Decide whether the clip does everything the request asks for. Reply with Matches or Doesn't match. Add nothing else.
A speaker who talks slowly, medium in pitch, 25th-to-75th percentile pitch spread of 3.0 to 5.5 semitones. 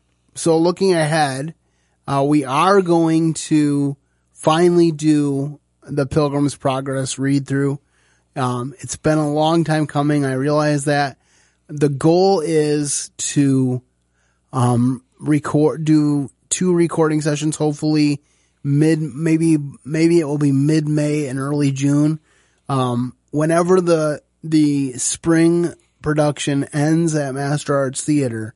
Doesn't match